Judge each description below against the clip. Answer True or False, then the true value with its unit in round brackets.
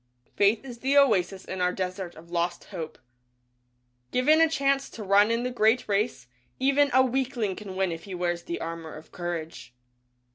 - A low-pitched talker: False (200 Hz)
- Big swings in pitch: True (6.4 semitones)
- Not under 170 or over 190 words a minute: True (180 wpm)